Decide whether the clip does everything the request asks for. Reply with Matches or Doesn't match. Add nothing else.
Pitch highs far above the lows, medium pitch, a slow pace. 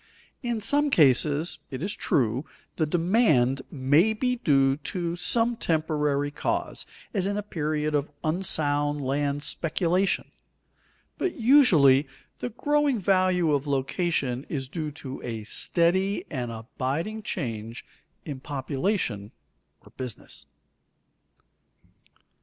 Matches